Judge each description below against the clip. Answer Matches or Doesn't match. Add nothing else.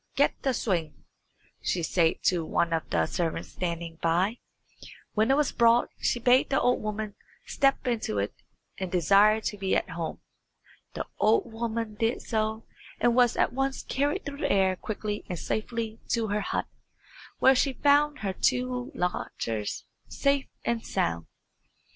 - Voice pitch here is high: Matches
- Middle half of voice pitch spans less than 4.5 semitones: Doesn't match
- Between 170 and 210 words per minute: Doesn't match